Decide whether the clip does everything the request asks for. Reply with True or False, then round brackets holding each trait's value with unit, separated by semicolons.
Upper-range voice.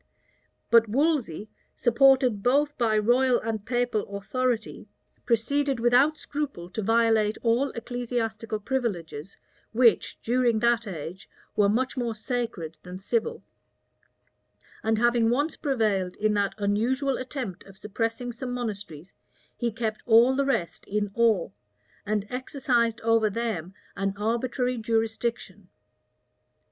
True (230 Hz)